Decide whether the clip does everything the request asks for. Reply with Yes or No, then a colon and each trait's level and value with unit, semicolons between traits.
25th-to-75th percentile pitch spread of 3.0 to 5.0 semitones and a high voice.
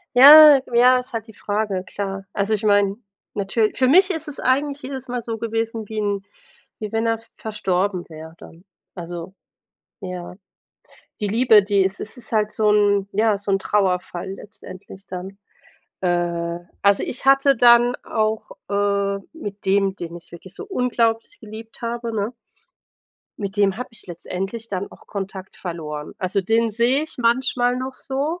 Yes: average, 3.6 semitones; high, 210 Hz